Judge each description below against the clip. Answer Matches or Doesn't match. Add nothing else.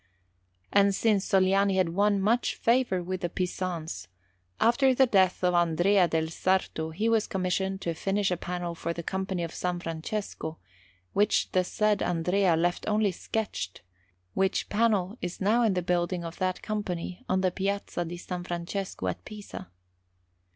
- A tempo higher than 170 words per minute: Doesn't match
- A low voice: Doesn't match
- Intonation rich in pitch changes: Doesn't match